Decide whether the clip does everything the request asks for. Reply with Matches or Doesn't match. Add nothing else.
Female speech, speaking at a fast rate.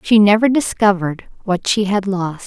Doesn't match